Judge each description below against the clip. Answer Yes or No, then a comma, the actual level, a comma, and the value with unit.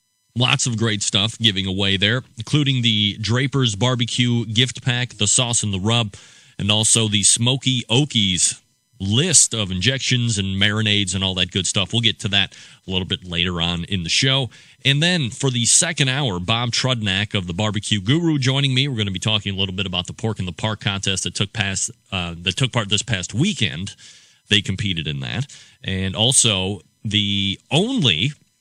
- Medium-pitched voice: No, low, 110 Hz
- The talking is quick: No, average, 190 wpm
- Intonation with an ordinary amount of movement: Yes, average, 4.2 semitones